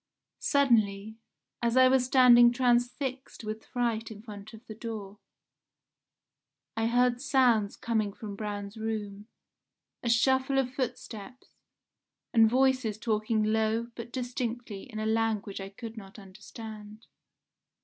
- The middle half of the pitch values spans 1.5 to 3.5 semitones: Yes, narrow, 2.5 semitones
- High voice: Yes, high, 225 Hz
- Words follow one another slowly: Yes, slow, 125 wpm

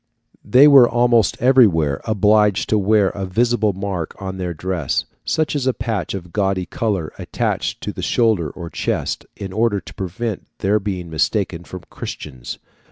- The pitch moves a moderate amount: Yes, average, 4.0 semitones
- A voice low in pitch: Yes, low, 100 Hz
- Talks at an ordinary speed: Yes, average, 165 wpm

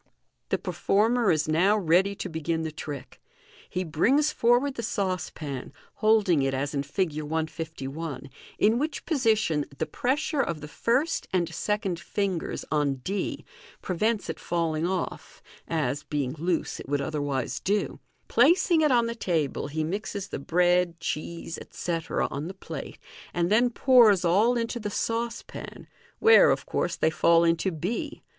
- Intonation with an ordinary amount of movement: No, wide, 5.7 semitones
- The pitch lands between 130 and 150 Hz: No, medium, 175 Hz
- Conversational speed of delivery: Yes, average, 155 wpm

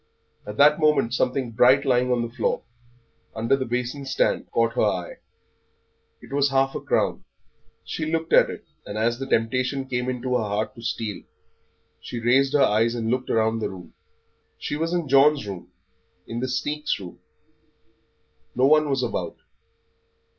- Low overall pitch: Yes, low, 125 Hz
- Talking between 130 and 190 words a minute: Yes, average, 170 wpm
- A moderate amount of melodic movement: Yes, average, 3.3 semitones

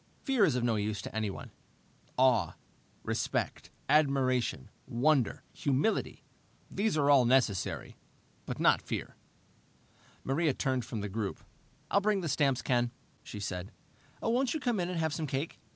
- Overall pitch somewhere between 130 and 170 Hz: Yes, low, 135 Hz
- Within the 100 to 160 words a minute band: Yes, average, 150 wpm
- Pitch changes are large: Yes, wide, 5.7 semitones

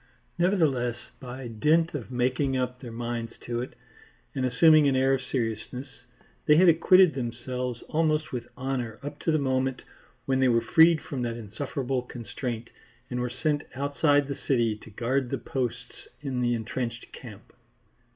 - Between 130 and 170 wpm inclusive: Yes, average, 160 wpm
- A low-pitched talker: Yes, low, 130 Hz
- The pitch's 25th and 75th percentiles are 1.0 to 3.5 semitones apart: Yes, average, 3.0 semitones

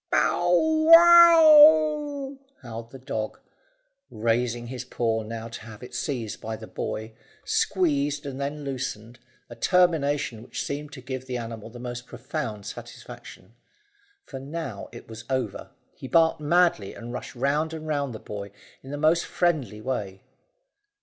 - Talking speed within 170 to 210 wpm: No, average, 150 wpm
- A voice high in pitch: No, low, 130 Hz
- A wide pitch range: Yes, wide, 5.9 semitones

